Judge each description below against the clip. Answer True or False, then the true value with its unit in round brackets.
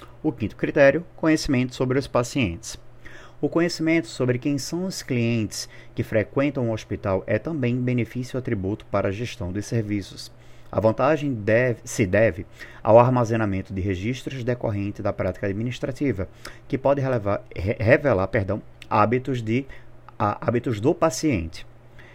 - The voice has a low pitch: True (120 Hz)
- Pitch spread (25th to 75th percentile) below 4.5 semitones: True (3.6 semitones)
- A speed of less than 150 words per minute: True (135 wpm)